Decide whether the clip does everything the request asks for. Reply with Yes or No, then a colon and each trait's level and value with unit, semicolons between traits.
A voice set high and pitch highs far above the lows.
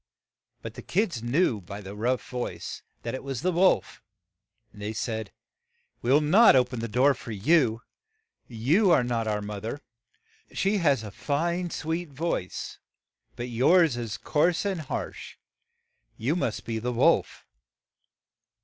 No: low, 125 Hz; wide, 6.6 semitones